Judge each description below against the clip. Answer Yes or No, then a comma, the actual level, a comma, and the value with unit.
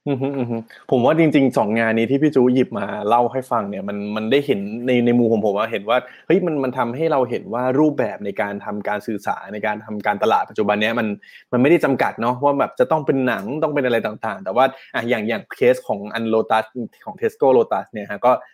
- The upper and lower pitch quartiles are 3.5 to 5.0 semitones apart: Yes, average, 4.0 semitones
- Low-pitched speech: Yes, low, 120 Hz